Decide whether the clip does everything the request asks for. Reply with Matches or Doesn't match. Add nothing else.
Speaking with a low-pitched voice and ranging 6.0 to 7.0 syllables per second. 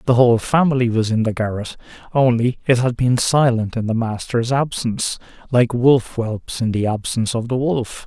Doesn't match